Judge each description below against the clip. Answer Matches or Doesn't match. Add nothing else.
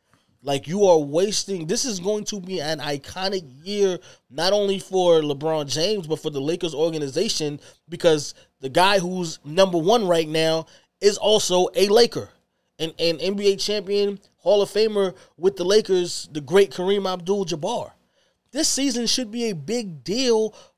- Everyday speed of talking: Matches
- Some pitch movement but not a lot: Matches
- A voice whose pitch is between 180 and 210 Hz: Matches